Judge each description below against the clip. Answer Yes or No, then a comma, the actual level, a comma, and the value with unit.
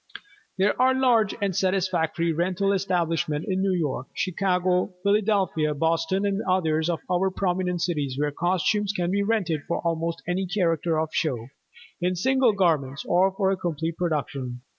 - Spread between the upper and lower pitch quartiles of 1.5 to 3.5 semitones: Yes, average, 3.0 semitones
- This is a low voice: No, medium, 180 Hz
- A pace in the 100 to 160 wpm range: Yes, average, 155 wpm